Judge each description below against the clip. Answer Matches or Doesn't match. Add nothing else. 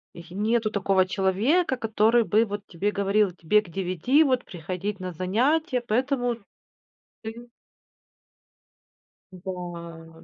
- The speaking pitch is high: Matches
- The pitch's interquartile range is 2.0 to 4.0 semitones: Doesn't match